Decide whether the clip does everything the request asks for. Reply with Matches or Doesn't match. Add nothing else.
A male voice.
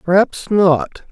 Matches